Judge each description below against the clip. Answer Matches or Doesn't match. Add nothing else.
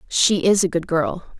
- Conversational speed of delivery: Doesn't match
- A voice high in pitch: Doesn't match